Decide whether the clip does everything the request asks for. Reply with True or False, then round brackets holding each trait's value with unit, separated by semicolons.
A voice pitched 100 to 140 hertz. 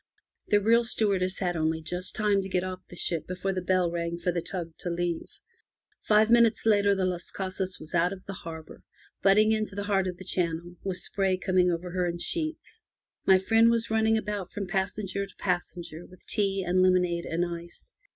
False (185 Hz)